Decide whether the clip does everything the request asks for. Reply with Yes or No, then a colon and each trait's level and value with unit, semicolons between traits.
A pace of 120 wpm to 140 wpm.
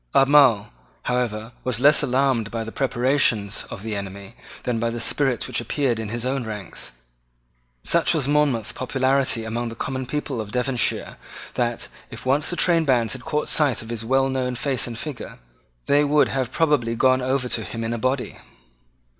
No: average, 180 wpm